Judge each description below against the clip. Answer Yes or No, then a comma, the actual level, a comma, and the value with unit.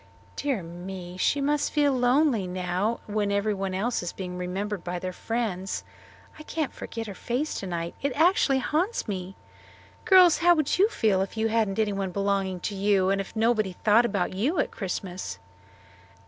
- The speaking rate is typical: Yes, average, 170 wpm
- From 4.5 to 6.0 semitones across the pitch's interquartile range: Yes, average, 4.9 semitones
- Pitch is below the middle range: No, high, 205 Hz